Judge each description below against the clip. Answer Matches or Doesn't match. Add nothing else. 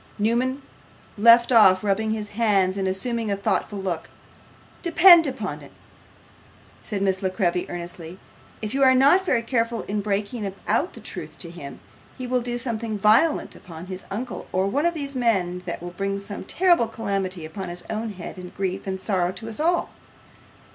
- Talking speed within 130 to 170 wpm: Doesn't match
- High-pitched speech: Matches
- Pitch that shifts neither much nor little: Matches